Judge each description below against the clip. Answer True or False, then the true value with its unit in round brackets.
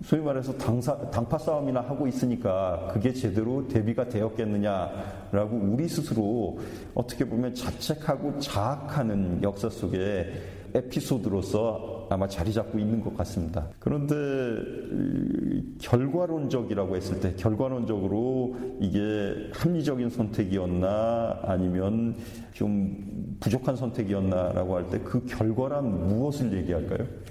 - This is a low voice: True (115 Hz)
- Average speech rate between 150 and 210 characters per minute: False (290 characters per minute)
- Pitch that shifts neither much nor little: True (4.3 semitones)